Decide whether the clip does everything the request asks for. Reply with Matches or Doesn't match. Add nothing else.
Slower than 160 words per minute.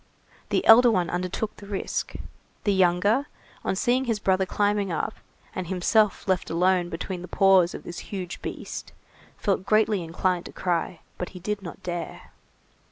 Doesn't match